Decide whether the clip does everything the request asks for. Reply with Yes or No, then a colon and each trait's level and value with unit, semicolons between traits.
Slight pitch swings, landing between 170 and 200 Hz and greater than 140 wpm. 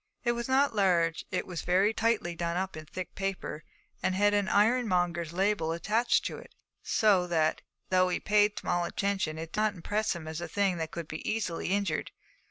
No: average, 3.5 semitones; medium, 185 Hz; average, 185 wpm